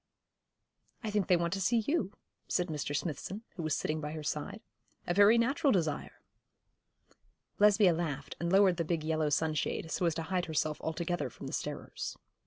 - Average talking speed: Yes, average, 180 wpm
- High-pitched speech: No, medium, 170 Hz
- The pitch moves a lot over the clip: No, average, 4.1 semitones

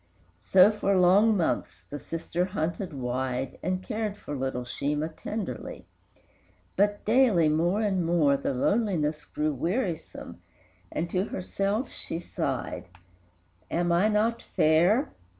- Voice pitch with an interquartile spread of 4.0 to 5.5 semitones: Yes, average, 5.2 semitones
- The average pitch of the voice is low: No, medium, 175 Hz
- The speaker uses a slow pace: Yes, slow, 125 wpm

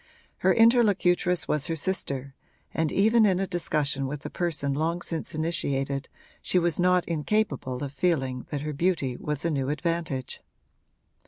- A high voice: No, medium, 160 Hz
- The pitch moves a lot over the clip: No, average, 4.3 semitones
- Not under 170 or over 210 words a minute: No, average, 155 wpm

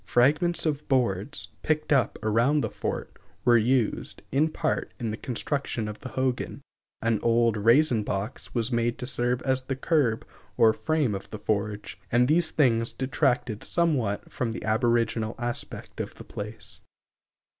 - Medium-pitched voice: No, low, 120 Hz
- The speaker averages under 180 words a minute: Yes, average, 155 wpm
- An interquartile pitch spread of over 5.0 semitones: No, average, 3.7 semitones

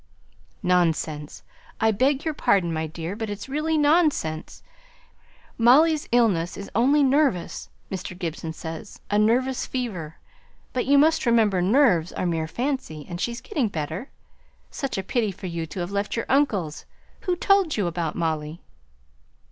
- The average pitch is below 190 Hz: No, high, 205 Hz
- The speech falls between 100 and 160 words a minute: Yes, average, 150 wpm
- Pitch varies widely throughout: Yes, wide, 8.1 semitones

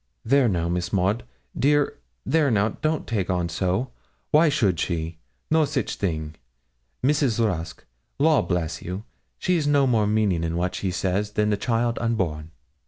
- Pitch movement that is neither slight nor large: No, wide, 7.2 semitones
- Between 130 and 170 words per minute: Yes, average, 165 wpm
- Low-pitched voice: Yes, low, 105 Hz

